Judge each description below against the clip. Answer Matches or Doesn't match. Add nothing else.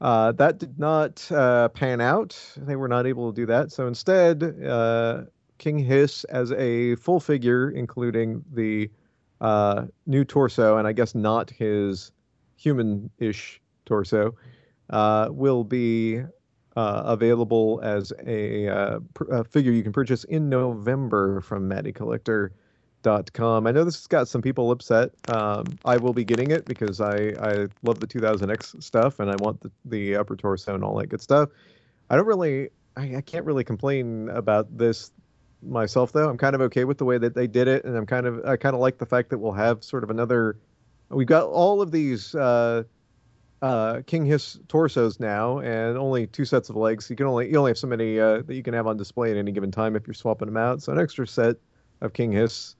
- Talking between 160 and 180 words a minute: Doesn't match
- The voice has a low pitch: Matches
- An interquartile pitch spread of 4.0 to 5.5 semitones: Doesn't match